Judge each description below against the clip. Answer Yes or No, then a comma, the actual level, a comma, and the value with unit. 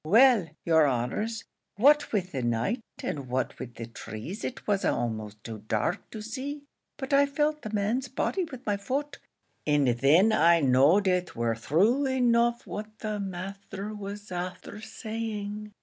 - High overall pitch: Yes, high, 205 Hz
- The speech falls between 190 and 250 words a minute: No, average, 160 wpm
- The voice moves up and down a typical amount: No, wide, 7.8 semitones